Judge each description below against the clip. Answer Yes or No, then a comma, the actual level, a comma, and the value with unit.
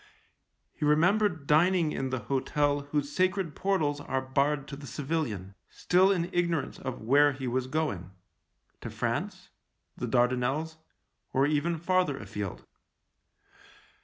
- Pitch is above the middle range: No, medium, 145 Hz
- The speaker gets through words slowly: Yes, slow, 130 wpm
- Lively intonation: No, average, 4.0 semitones